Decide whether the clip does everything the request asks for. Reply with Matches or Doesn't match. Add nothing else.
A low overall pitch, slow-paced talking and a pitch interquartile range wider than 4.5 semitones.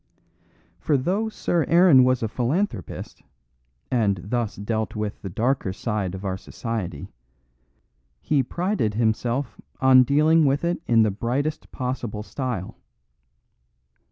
Matches